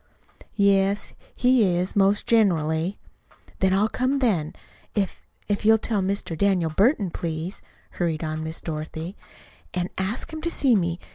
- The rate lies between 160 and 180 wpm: No, average, 145 wpm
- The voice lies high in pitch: Yes, high, 195 Hz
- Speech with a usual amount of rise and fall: Yes, average, 4.2 semitones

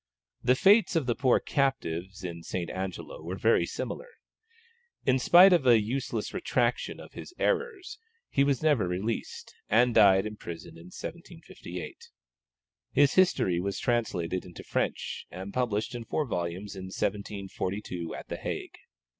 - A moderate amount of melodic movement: No, wide, 6.7 semitones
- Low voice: Yes, low, 110 Hz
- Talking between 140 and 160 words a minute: Yes, average, 145 wpm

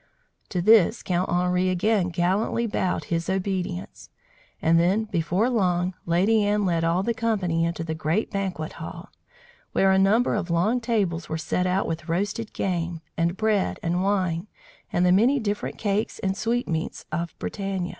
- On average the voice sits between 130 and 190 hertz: Yes, medium, 185 Hz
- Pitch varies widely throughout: No, average, 3.4 semitones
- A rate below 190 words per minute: Yes, average, 165 wpm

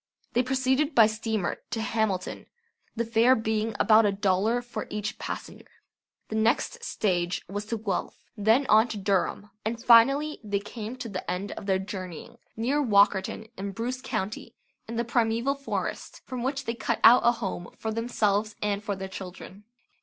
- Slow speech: No, average, 170 wpm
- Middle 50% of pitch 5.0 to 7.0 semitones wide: No, average, 2.8 semitones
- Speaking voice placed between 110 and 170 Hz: No, high, 220 Hz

